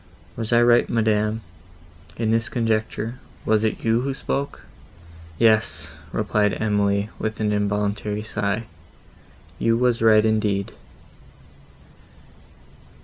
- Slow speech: Yes, slow, 100 wpm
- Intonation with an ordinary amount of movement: No, narrow, 1.7 semitones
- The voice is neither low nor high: No, low, 110 Hz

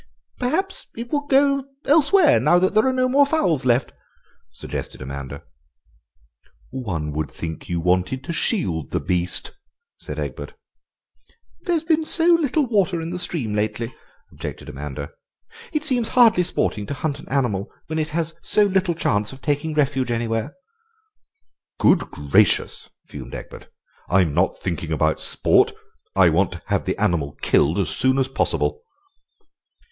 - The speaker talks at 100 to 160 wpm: Yes, average, 150 wpm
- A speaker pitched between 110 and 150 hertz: Yes, low, 135 Hz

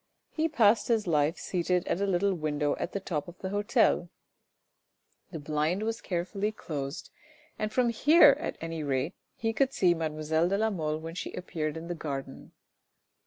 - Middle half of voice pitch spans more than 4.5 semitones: Yes, average, 5.0 semitones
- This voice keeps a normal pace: Yes, average, 170 wpm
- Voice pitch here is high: No, medium, 175 Hz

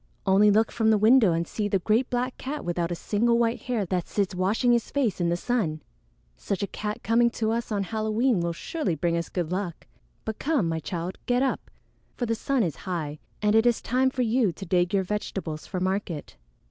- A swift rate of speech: Yes, fast, 220 wpm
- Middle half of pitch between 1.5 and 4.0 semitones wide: No, average, 5.0 semitones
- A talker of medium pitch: No, high, 210 Hz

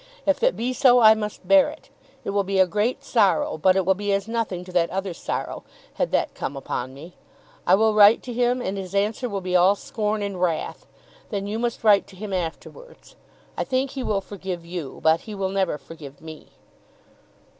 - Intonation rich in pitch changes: No, average, 3.3 semitones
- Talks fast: Yes, fast, 210 wpm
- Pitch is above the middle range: Yes, high, 195 Hz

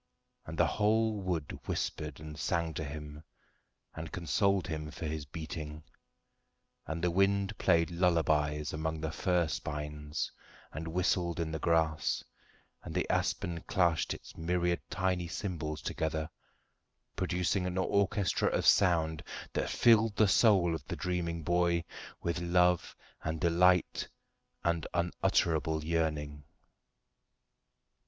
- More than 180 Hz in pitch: No, very low, 85 Hz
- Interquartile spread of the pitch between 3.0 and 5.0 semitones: No, narrow, 2.6 semitones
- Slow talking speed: Yes, slow, 125 wpm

